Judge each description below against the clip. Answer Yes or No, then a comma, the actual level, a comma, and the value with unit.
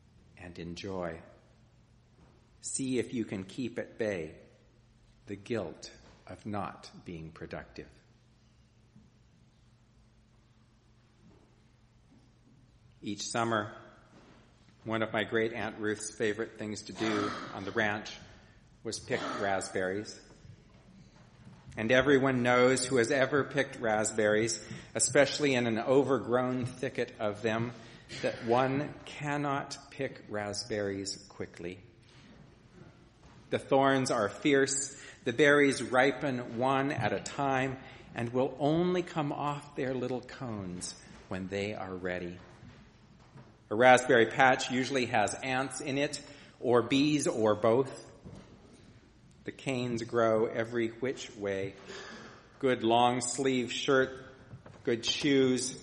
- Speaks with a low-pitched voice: Yes, low, 120 Hz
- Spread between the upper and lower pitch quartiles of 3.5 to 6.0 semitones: No, average, 3.1 semitones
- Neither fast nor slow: No, slow, 110 wpm